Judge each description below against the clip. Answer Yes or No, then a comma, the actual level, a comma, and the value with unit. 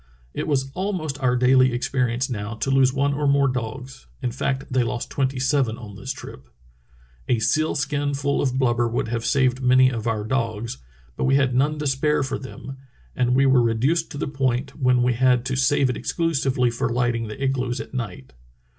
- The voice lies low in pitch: Yes, low, 130 Hz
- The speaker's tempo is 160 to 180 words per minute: No, average, 200 wpm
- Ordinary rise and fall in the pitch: No, narrow, 2.2 semitones